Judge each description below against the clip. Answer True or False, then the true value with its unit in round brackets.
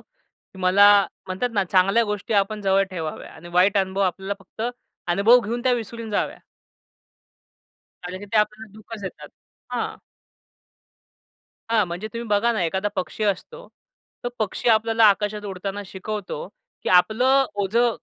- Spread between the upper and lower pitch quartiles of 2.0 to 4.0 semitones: True (2.8 semitones)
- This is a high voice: True (205 Hz)